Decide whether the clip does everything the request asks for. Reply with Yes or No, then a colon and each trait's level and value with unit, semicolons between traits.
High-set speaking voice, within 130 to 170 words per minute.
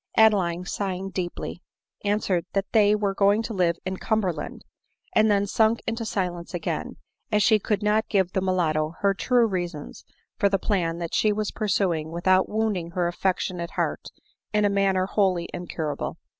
Yes: high, 195 Hz; average, 165 wpm